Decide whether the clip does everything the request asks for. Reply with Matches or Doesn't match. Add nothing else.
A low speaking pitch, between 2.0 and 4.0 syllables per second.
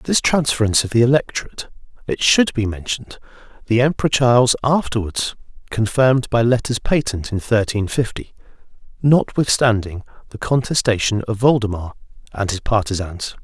Doesn't match